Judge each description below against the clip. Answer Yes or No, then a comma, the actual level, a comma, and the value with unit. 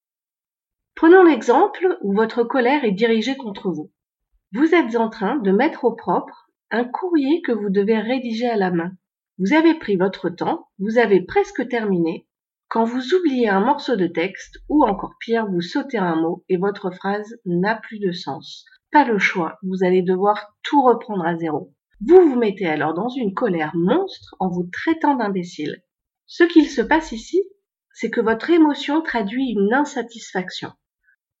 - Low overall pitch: No, high, 225 Hz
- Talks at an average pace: Yes, average, 170 wpm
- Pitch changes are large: Yes, wide, 7.5 semitones